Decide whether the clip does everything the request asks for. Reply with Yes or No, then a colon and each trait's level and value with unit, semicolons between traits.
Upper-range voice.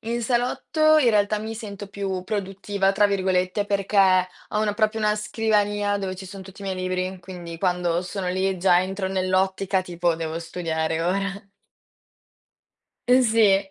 Yes: high, 195 Hz